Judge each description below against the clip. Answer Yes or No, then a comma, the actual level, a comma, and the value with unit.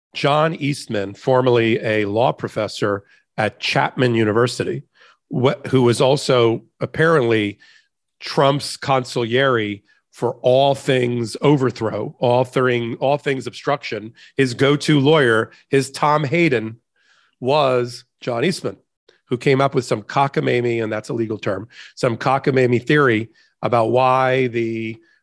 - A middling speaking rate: No, slow, 120 wpm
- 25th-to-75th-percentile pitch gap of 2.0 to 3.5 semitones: Yes, average, 3.0 semitones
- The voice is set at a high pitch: No, low, 125 Hz